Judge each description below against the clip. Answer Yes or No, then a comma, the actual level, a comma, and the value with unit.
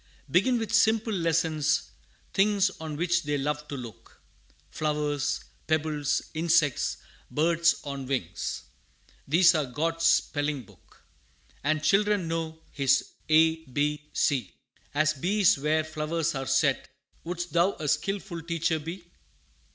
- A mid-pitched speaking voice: Yes, medium, 155 Hz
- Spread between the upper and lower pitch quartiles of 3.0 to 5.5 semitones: No, narrow, 2.6 semitones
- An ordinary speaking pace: No, slow, 125 wpm